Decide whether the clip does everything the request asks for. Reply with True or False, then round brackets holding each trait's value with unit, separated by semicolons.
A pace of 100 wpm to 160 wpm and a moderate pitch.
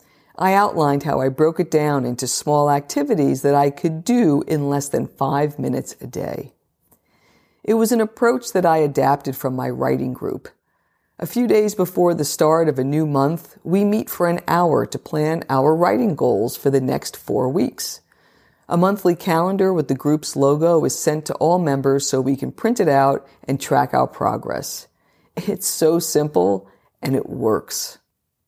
False (180 wpm; 155 Hz)